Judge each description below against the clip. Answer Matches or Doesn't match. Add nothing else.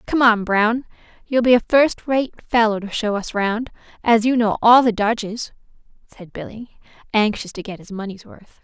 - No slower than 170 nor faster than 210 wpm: Matches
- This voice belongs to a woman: Matches